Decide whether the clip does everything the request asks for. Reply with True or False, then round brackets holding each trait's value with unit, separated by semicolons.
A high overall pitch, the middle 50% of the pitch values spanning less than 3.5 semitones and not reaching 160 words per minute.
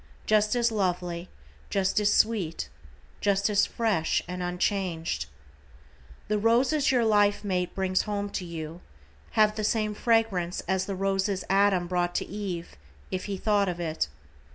True (195 Hz; 2.9 semitones; 150 wpm)